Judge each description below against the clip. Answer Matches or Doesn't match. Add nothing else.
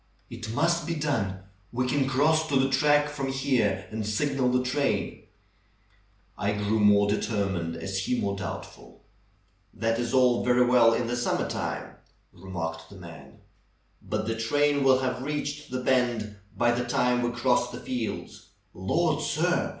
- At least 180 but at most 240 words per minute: Doesn't match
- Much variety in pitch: Doesn't match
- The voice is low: Matches